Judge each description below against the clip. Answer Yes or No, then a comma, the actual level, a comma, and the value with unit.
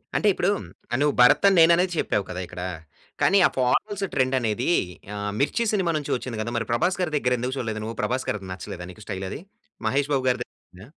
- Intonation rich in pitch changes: Yes, wide, 6.7 semitones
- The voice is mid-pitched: No, low, 125 Hz